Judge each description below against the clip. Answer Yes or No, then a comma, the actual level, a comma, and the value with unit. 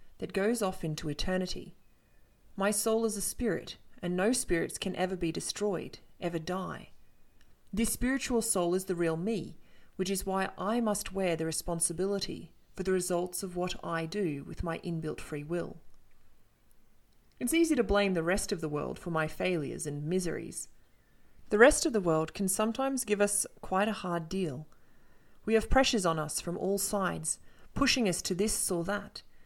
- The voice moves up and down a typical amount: Yes, average, 3.5 semitones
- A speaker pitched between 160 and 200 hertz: Yes, high, 190 Hz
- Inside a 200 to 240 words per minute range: No, average, 175 wpm